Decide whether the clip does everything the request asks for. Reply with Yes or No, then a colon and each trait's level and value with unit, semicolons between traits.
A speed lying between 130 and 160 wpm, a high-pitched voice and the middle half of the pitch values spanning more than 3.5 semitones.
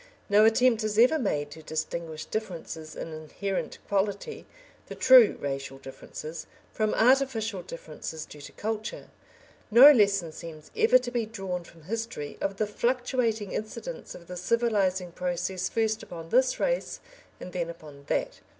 Yes: average, 150 wpm; high, 200 Hz; wide, 5.5 semitones